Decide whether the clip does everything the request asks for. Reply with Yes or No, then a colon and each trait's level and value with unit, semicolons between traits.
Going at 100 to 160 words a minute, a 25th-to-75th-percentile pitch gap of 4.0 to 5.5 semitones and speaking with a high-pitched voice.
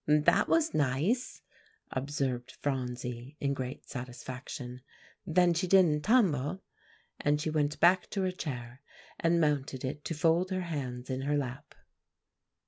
No: slow, 135 wpm; average, 4.7 semitones; medium, 145 Hz